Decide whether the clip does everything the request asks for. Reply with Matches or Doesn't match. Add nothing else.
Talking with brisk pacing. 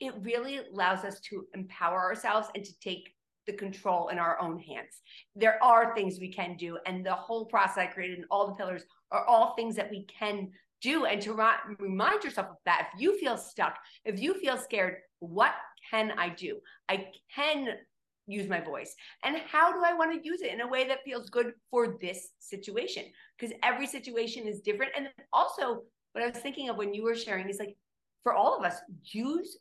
Matches